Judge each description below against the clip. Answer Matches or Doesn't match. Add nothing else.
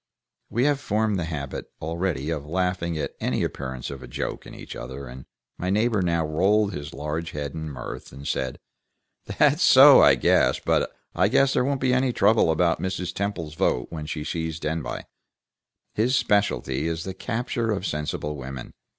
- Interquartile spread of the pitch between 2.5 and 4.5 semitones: Doesn't match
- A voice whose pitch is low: Matches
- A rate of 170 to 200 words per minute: Matches